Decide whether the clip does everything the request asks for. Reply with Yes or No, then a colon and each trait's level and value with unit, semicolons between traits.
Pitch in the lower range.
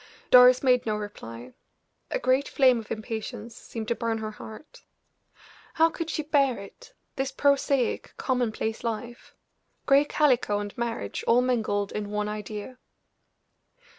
No: high, 235 Hz